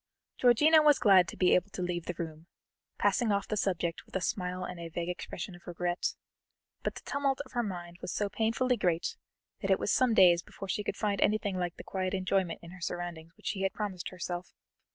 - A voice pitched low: No, medium, 185 Hz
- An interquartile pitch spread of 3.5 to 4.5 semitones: No, average, 3.1 semitones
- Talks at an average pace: No, fast, 220 wpm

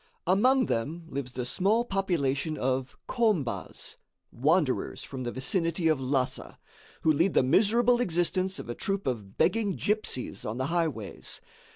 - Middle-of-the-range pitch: Yes, medium, 165 Hz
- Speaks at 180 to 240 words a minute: No, average, 145 wpm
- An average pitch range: No, wide, 7.0 semitones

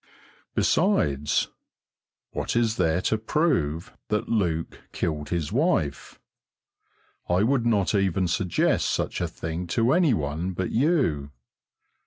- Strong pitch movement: Yes, wide, 6.2 semitones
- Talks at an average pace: No, slow, 120 wpm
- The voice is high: No, very low, 90 Hz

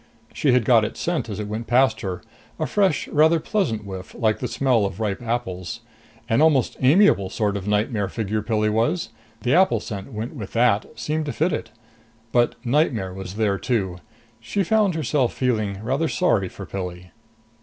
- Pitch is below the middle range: Yes, low, 115 Hz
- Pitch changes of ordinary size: No, wide, 5.7 semitones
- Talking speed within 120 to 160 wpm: No, average, 180 wpm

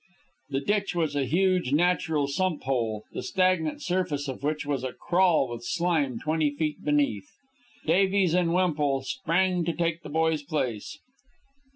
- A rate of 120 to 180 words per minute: Yes, average, 155 wpm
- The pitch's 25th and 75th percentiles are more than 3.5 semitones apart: Yes, average, 4.1 semitones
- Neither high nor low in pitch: Yes, medium, 155 Hz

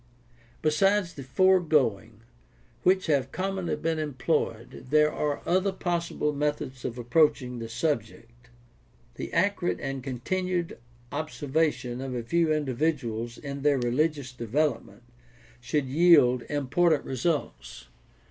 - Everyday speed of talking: No, slow, 115 wpm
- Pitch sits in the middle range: Yes, medium, 145 Hz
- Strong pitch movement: No, average, 5.0 semitones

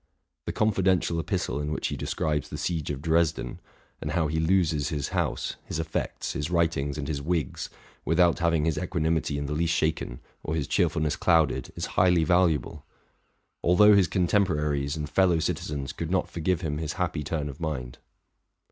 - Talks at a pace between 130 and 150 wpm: No, average, 175 wpm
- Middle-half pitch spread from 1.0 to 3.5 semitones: Yes, average, 2.7 semitones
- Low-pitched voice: Yes, very low, 80 Hz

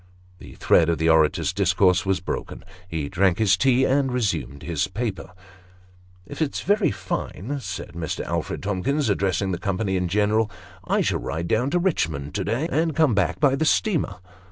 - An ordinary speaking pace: Yes, average, 185 wpm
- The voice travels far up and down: Yes, wide, 6.8 semitones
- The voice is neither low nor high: No, low, 100 Hz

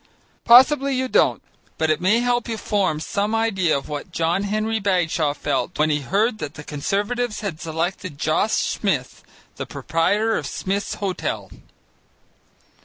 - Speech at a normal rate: Yes, average, 150 wpm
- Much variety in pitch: Yes, wide, 5.8 semitones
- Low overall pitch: No, high, 195 Hz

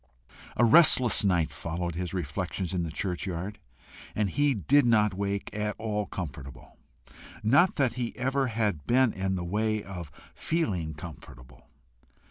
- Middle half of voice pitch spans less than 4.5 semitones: No, average, 5.1 semitones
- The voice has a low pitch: Yes, low, 100 Hz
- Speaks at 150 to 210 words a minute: No, average, 140 wpm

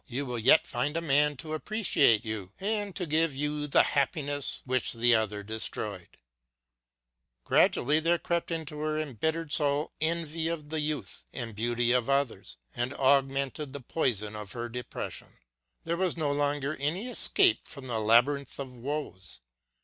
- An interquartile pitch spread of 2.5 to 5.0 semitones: Yes, average, 4.6 semitones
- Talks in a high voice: No, medium, 140 Hz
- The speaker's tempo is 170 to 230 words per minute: No, average, 160 wpm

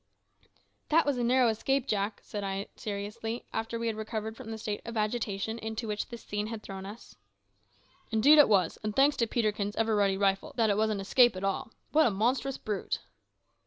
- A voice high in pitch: Yes, high, 220 Hz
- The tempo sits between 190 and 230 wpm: Yes, average, 200 wpm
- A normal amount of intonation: No, narrow, 2.3 semitones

